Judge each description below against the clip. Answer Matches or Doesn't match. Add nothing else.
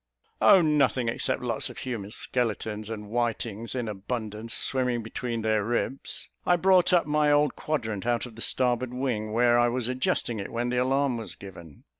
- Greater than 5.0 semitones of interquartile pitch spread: Doesn't match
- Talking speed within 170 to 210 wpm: Matches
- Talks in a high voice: Doesn't match